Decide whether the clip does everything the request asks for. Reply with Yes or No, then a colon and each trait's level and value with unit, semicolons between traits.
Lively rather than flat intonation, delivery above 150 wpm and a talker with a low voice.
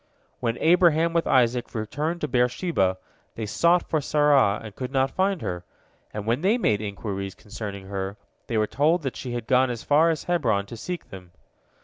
Yes: wide, 7.2 semitones; average, 195 wpm; low, 125 Hz